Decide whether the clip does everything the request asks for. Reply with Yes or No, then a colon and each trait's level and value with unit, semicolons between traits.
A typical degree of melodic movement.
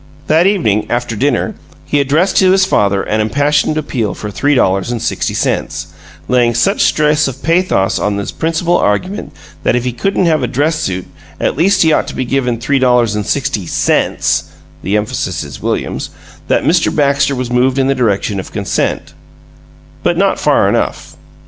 No: wide, 5.9 semitones